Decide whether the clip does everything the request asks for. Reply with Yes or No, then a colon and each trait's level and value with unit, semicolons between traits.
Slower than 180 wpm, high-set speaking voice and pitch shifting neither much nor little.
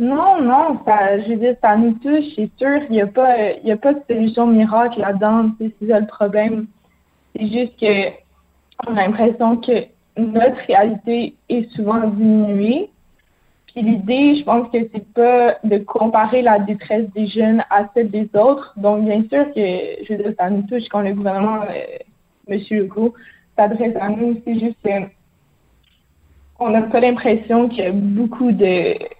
No: average, 170 wpm; high, 220 Hz; narrow, 2.3 semitones